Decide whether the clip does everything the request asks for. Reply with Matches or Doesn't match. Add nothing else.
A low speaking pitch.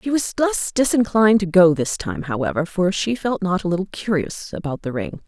Doesn't match